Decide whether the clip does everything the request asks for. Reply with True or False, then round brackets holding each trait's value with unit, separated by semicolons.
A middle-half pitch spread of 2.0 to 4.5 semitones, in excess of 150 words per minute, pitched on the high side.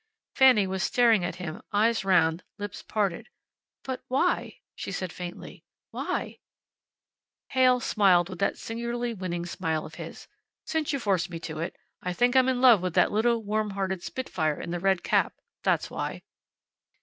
False (5.2 semitones; 160 wpm; 200 Hz)